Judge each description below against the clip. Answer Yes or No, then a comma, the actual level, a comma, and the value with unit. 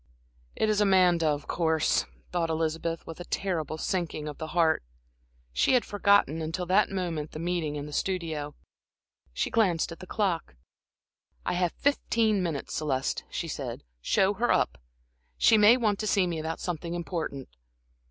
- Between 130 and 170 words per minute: Yes, average, 160 wpm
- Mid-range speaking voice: Yes, medium, 170 Hz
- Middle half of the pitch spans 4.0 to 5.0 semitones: No, average, 3.6 semitones